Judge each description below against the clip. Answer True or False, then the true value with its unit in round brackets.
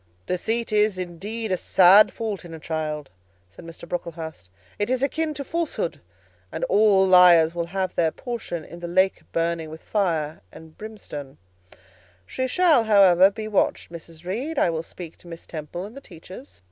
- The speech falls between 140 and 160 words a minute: False (170 wpm)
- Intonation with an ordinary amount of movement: True (4.6 semitones)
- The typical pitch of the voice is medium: True (180 Hz)